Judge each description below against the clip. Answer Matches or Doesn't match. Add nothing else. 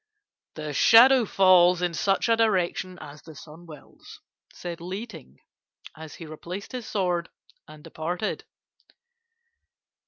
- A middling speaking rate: Doesn't match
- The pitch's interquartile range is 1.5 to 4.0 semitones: Matches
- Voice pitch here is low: Doesn't match